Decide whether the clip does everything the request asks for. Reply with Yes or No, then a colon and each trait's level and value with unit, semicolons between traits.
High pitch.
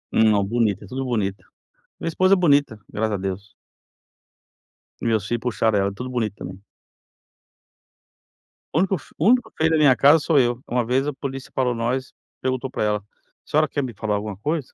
No: low, 125 Hz